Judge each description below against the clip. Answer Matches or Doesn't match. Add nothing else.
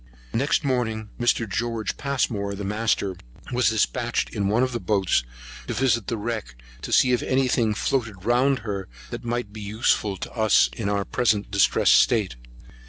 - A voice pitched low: Matches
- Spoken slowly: Doesn't match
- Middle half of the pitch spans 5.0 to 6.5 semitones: Doesn't match